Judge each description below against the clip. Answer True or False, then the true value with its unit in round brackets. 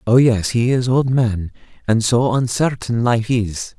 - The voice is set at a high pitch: False (115 Hz)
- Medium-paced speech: True (160 wpm)